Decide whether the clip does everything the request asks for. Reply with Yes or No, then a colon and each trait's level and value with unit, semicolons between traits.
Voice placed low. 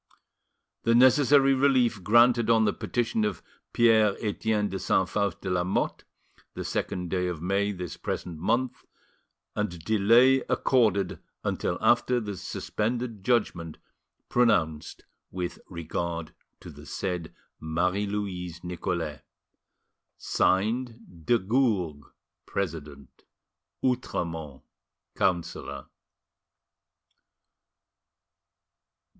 Yes: low, 100 Hz